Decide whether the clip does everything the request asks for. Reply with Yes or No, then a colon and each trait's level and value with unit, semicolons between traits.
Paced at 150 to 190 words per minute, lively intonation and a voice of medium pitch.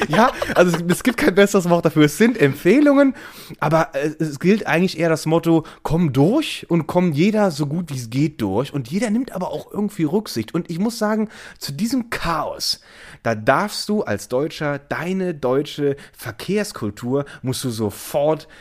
Yes: average, 175 wpm; wide, 6.0 semitones; medium, 165 Hz